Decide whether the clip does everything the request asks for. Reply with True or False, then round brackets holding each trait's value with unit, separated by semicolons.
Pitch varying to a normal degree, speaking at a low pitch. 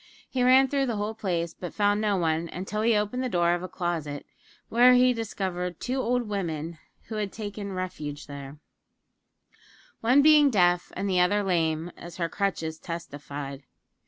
False (4.8 semitones; 185 Hz)